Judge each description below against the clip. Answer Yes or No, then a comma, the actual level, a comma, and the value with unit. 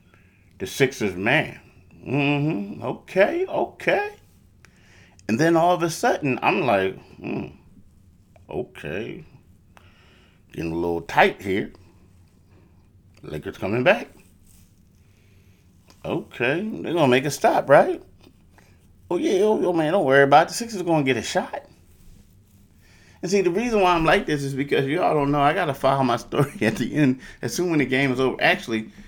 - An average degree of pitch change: No, wide, 7.9 semitones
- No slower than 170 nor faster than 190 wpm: No, average, 160 wpm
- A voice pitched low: Yes, low, 100 Hz